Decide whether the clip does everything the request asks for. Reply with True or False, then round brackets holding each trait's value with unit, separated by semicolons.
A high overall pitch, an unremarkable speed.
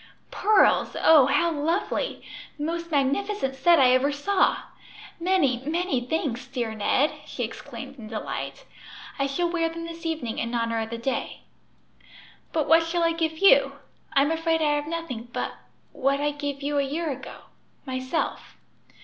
True (290 Hz; 160 wpm)